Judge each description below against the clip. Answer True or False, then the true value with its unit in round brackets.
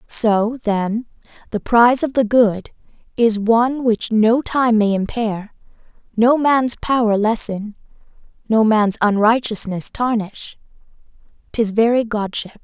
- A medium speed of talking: False (120 wpm)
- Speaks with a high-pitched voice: True (225 Hz)